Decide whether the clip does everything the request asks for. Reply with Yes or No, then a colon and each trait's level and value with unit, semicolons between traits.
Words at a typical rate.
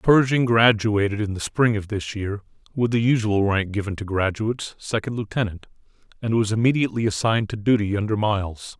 Yes: average, 170 wpm